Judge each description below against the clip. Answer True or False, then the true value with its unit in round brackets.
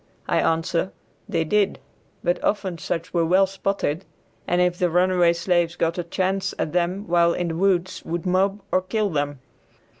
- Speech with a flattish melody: True (2.0 semitones)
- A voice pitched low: False (180 Hz)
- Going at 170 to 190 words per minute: True (175 wpm)